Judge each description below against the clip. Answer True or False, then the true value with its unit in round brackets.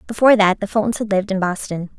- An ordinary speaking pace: False (240 wpm)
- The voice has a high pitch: True (200 Hz)